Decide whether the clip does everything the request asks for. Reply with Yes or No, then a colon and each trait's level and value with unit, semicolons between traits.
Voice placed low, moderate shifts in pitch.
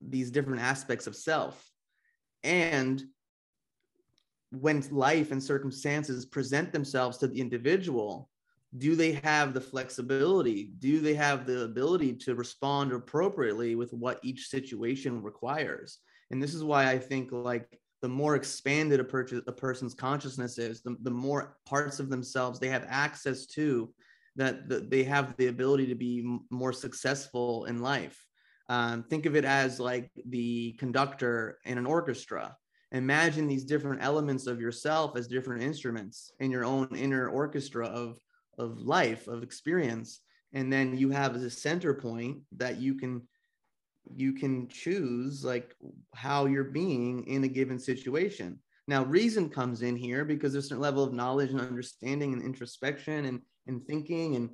No: low, 130 Hz; narrow, 2.3 semitones